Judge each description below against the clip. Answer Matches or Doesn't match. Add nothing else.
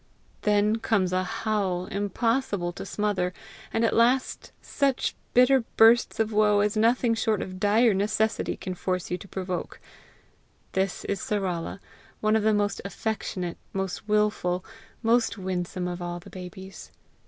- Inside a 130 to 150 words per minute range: Matches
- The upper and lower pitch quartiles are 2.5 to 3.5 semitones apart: Matches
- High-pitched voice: Matches